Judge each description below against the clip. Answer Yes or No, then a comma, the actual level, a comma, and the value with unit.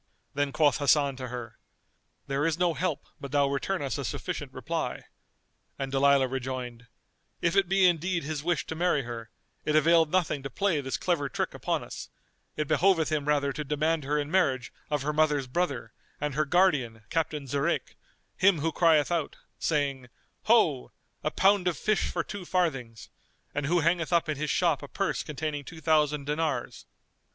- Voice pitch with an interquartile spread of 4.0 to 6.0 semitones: No, average, 3.3 semitones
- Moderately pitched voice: Yes, medium, 150 Hz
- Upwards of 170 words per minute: Yes, average, 180 wpm